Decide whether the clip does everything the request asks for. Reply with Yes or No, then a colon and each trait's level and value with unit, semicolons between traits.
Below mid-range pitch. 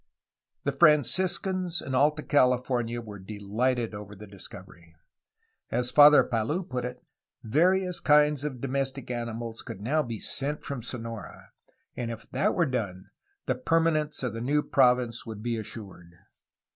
Yes: low, 125 Hz